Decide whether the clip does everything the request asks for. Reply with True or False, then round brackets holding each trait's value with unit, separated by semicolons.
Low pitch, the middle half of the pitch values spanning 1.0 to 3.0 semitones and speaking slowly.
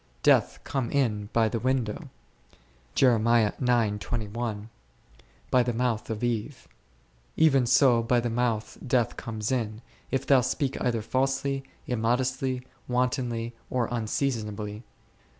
True (120 Hz; 2.5 semitones; 115 wpm)